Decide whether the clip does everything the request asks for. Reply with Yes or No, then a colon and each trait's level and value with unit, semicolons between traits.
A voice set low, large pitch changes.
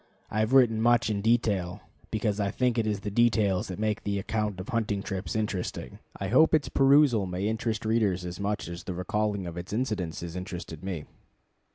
No: low, 105 Hz; average, 3.4 semitones